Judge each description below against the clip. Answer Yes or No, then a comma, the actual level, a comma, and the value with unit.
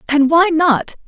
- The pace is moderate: Yes, average, 170 wpm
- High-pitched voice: Yes, very high, 310 Hz